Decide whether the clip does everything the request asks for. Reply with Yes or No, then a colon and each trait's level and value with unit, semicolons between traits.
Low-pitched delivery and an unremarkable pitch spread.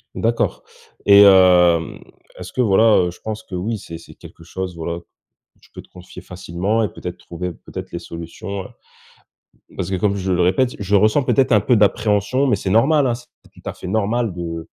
Yes: very low, 95 Hz; average, 3.7 semitones